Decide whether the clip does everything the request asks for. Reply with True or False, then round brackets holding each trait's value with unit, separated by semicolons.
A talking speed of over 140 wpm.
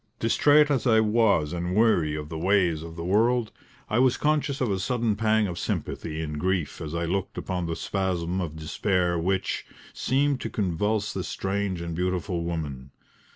True (180 wpm)